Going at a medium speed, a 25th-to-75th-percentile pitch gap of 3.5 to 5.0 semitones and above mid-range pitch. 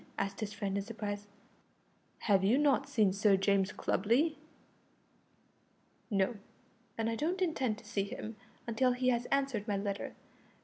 Yes: average, 145 wpm; average, 4.0 semitones; high, 215 Hz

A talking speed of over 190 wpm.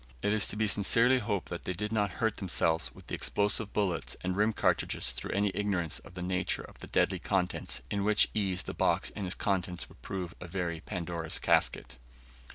Yes: fast, 205 wpm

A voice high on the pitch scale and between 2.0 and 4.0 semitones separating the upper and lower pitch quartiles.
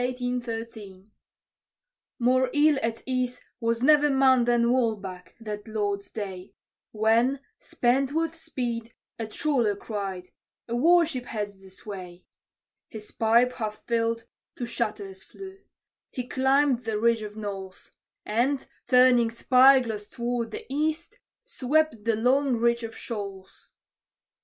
Yes: high, 235 Hz; average, 3.4 semitones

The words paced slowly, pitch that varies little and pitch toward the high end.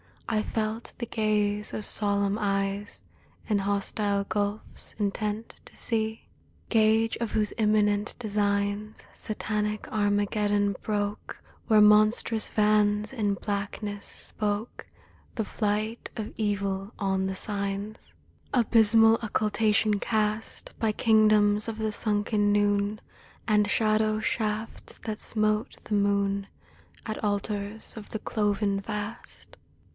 Yes: slow, 115 wpm; narrow, 1.1 semitones; high, 210 Hz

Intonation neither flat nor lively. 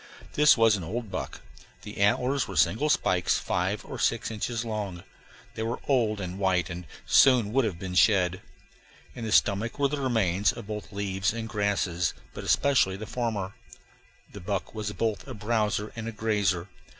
Yes: average, 3.2 semitones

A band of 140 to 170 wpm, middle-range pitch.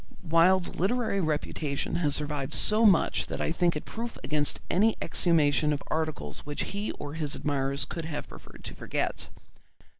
Yes: average, 160 wpm; medium, 160 Hz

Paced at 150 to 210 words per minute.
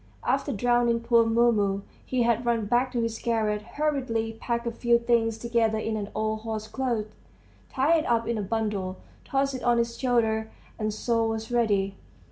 Yes: average, 175 wpm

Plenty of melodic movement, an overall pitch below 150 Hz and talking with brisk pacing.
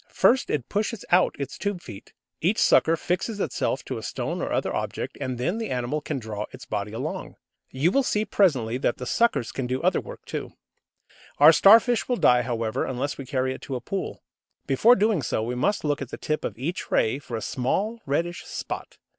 Yes: wide, 8.0 semitones; medium, 140 Hz; fast, 210 wpm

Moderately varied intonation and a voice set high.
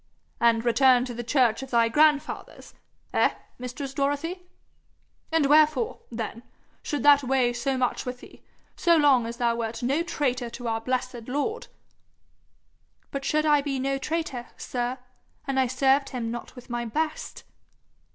Yes: average, 3.1 semitones; very high, 260 Hz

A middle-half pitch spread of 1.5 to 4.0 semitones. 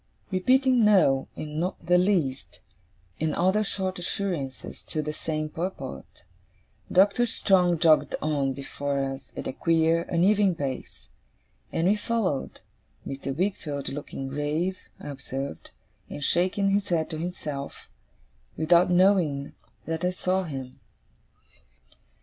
No: average, 4.8 semitones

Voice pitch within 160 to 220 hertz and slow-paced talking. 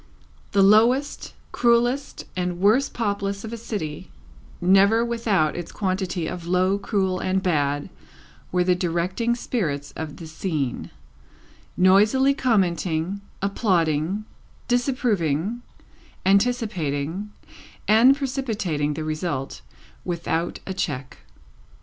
Yes: high, 190 Hz; slow, 100 wpm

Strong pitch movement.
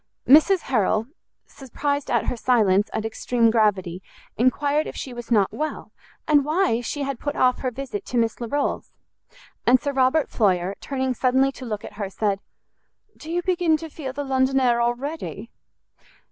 No: average, 4.1 semitones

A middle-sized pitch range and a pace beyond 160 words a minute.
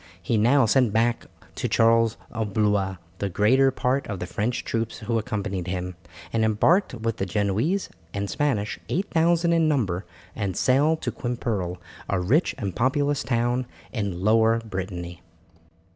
No: average, 4.4 semitones; average, 150 wpm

